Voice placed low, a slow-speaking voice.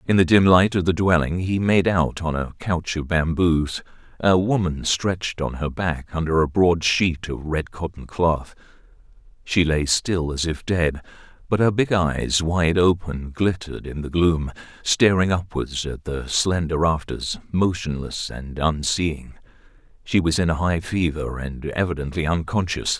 No: very low, 85 Hz; average, 165 wpm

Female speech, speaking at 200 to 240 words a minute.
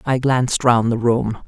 Yes: female; fast, 205 wpm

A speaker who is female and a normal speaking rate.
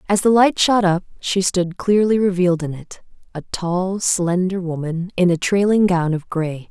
Yes: female; average, 180 wpm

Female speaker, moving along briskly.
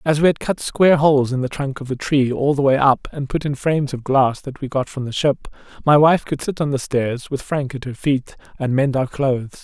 No: male; fast, 275 wpm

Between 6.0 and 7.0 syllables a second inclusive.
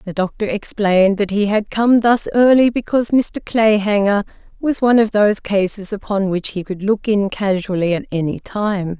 No: 5.0 syllables/s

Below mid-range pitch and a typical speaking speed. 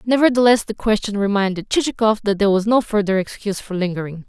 No: high, 210 Hz; average, 180 wpm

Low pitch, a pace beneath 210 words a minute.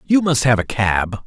No: low, 125 Hz; fast, 235 wpm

